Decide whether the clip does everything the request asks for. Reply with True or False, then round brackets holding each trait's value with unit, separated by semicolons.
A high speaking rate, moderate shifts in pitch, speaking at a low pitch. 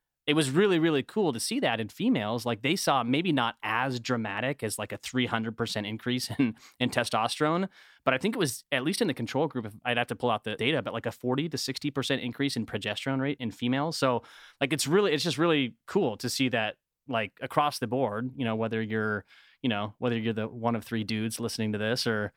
True (235 wpm; 3.3 semitones; 120 Hz)